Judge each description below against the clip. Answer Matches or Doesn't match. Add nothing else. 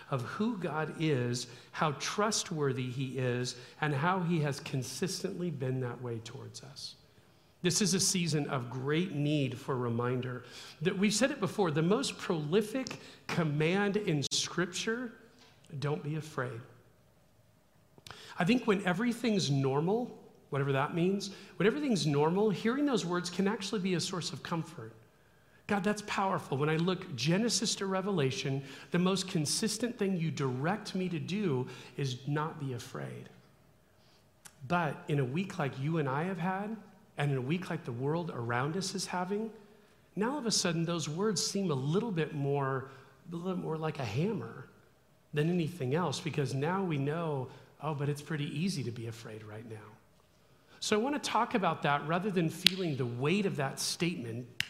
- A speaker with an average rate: Matches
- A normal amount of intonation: Doesn't match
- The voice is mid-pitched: Matches